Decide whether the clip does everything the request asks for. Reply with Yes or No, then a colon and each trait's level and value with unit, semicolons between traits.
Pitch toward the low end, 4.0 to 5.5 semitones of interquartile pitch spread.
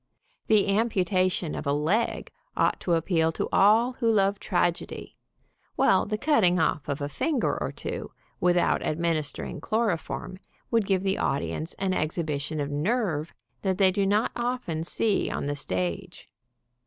No: medium, 185 Hz; average, 5.2 semitones